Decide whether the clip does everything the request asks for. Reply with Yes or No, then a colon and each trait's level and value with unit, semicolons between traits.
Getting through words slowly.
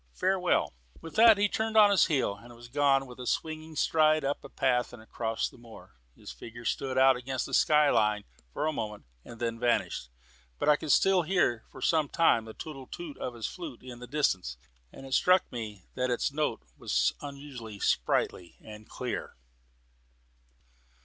No: average, 185 wpm